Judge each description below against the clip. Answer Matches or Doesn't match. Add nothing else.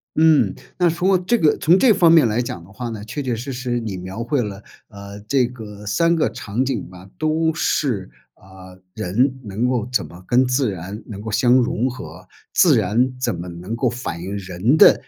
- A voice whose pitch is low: Matches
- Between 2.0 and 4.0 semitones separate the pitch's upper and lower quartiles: Doesn't match